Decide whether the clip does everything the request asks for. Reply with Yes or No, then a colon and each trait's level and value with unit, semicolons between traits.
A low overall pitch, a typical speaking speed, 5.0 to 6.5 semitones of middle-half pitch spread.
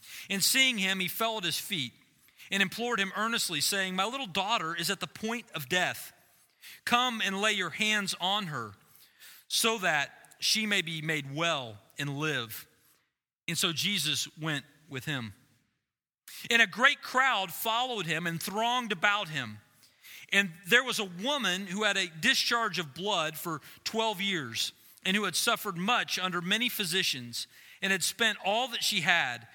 No: high, 195 Hz; average, 170 wpm; wide, 5.5 semitones